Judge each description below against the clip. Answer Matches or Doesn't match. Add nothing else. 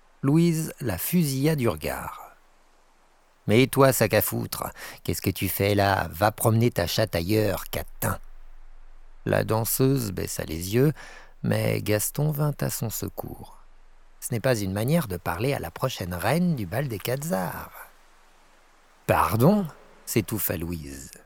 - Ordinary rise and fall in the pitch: Doesn't match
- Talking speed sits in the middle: Doesn't match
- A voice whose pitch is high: Doesn't match